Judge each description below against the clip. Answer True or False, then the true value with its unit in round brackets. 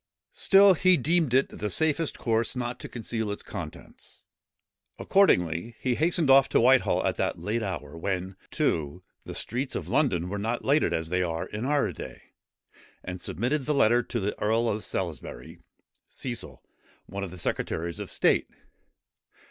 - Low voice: True (115 Hz)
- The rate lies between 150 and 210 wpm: True (165 wpm)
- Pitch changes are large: True (6.9 semitones)